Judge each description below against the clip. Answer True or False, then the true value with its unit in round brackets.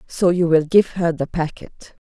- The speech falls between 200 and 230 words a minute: False (175 wpm)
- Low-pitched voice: False (170 Hz)